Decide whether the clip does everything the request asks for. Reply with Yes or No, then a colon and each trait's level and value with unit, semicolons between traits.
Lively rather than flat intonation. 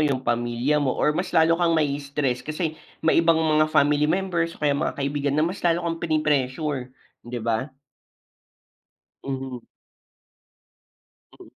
No: average, 3.3 semitones